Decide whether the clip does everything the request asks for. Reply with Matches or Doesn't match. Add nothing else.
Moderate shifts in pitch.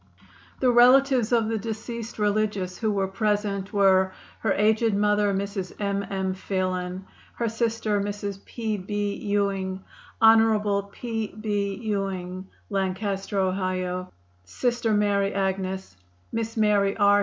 Doesn't match